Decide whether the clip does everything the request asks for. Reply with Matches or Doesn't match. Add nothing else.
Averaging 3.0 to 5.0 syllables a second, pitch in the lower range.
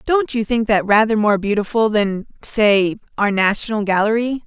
Doesn't match